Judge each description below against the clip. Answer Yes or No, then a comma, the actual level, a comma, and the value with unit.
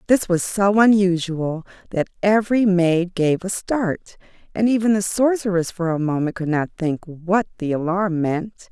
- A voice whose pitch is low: No, medium, 185 Hz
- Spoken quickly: No, average, 165 wpm